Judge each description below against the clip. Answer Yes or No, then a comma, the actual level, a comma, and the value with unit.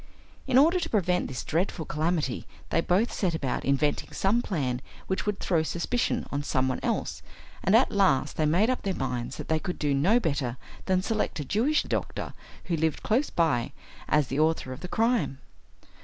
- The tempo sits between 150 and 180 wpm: No, average, 190 wpm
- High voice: No, medium, 165 Hz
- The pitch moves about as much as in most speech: No, wide, 6.4 semitones